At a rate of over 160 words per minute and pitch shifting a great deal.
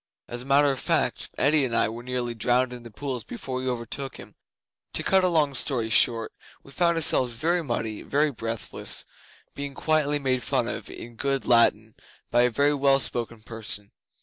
No: average, 190 wpm; average, 3.3 semitones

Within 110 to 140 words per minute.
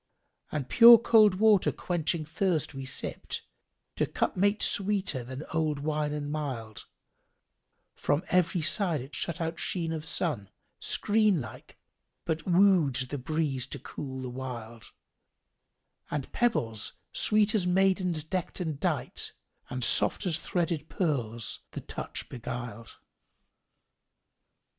Yes: slow, 135 wpm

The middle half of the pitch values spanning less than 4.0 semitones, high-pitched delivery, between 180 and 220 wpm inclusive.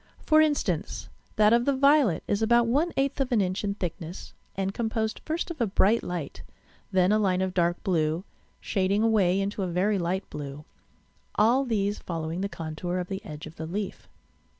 No: average, 4.4 semitones; high, 195 Hz; average, 190 wpm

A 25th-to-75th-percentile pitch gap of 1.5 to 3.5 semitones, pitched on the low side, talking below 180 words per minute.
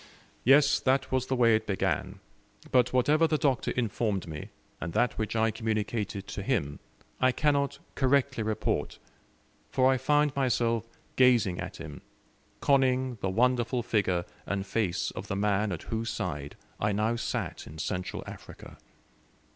No: average, 4.5 semitones; low, 115 Hz; average, 150 wpm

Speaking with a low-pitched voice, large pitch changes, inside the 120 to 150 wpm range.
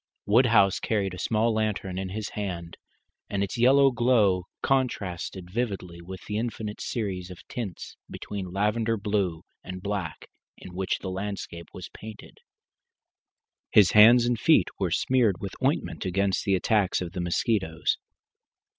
No: low, 100 Hz; average, 3.2 semitones; average, 145 wpm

